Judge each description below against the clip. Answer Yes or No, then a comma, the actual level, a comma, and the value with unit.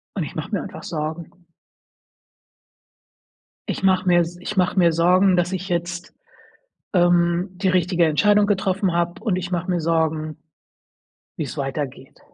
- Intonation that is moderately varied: No, narrow, 1.9 semitones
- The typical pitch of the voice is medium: Yes, medium, 175 Hz